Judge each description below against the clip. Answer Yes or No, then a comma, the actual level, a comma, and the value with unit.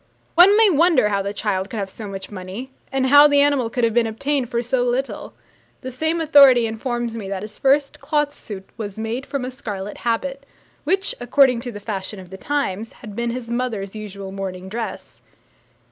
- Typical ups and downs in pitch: Yes, average, 5.0 semitones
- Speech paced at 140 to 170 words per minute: No, average, 200 wpm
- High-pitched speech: Yes, high, 235 Hz